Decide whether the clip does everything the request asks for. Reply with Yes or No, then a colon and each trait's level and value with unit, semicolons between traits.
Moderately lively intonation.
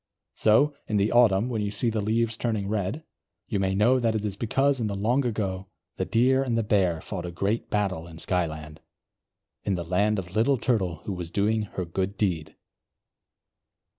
Yes: average, 3.6 semitones